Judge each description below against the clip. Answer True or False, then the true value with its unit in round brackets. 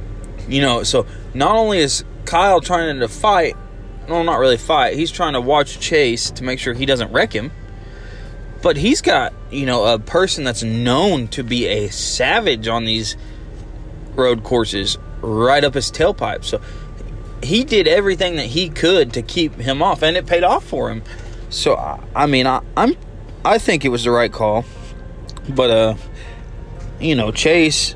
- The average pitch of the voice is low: True (120 Hz)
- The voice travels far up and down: True (5.8 semitones)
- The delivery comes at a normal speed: True (165 wpm)